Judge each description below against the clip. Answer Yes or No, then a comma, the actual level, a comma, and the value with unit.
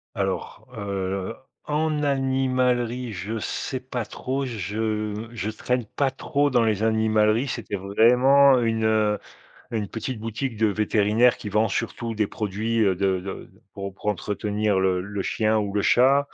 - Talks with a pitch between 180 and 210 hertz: No, low, 110 Hz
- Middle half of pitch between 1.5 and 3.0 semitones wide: No, average, 3.4 semitones